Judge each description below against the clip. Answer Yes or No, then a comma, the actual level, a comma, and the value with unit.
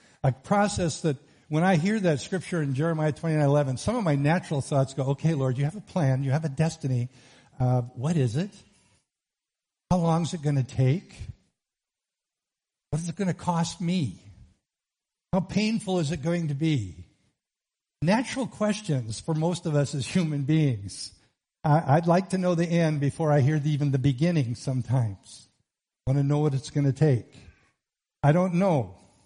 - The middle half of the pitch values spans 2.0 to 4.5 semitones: Yes, average, 4.2 semitones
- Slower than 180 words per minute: No, average, 185 wpm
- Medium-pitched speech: Yes, medium, 150 Hz